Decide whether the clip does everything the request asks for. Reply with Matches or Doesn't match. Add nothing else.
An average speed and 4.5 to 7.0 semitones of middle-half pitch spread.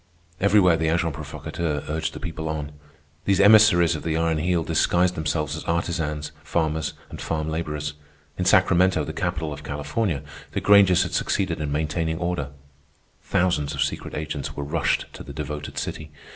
Doesn't match